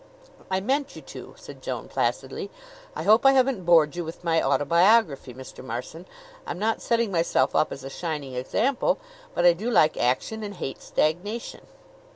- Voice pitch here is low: No, medium, 175 Hz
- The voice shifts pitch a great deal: Yes, wide, 6.8 semitones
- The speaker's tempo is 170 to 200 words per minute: Yes, average, 175 wpm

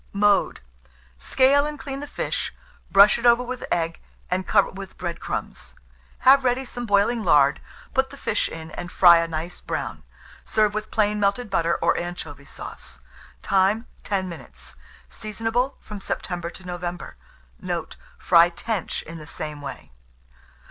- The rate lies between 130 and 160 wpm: Yes, average, 155 wpm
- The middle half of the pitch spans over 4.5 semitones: Yes, wide, 5.4 semitones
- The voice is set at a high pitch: Yes, high, 195 Hz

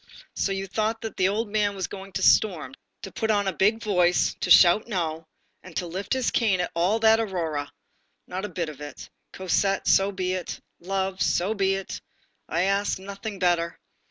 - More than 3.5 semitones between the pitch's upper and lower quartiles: No, narrow, 2.5 semitones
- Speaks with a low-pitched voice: No, high, 195 Hz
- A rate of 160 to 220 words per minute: Yes, average, 195 wpm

